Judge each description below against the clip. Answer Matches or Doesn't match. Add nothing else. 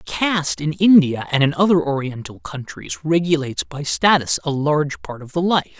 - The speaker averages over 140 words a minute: Matches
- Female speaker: Doesn't match